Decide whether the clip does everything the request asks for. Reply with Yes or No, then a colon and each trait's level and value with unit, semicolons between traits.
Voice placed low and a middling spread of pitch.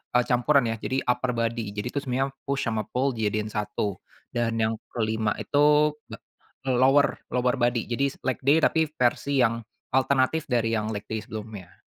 Yes: low, 120 Hz; average, 3.4 semitones